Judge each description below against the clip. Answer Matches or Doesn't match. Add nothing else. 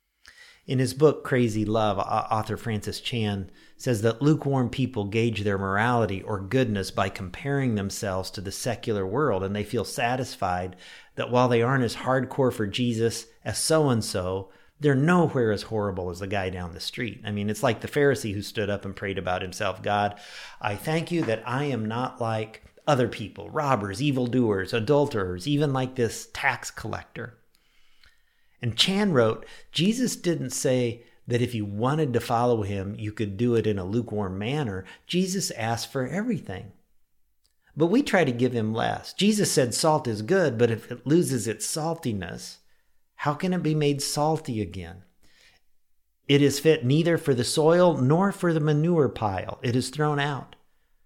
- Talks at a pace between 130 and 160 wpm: Doesn't match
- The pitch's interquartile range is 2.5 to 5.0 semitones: Doesn't match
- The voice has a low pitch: Matches